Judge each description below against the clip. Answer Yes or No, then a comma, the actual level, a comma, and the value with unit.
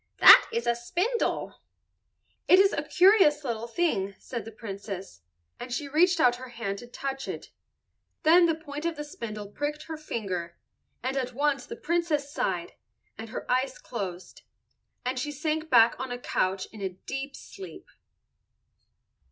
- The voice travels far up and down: Yes, wide, 5.7 semitones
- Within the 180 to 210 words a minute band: No, average, 160 wpm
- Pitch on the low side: No, very high, 255 Hz